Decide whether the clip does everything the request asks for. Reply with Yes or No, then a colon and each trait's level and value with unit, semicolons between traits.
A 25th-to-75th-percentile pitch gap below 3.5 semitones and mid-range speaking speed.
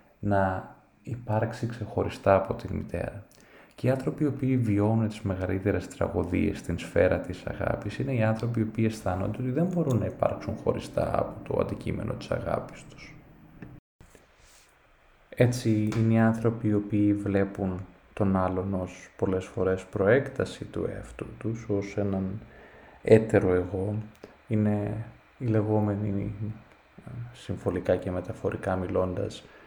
Yes: average, 2.8 semitones; average, 130 wpm